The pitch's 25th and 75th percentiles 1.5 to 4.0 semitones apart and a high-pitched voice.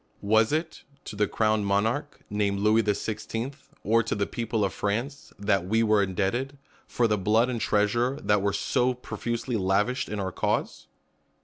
No: average, 2.8 semitones; low, 110 Hz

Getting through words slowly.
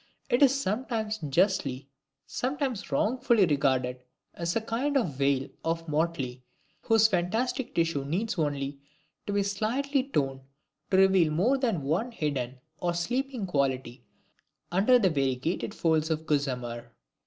Yes: slow, 130 wpm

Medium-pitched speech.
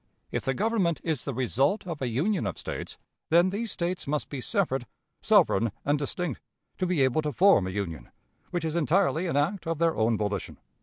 Yes: medium, 155 Hz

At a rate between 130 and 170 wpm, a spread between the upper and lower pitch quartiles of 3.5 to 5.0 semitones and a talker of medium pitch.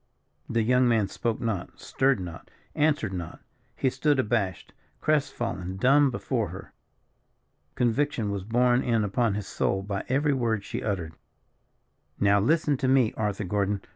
No: average, 150 wpm; average, 4.6 semitones; low, 115 Hz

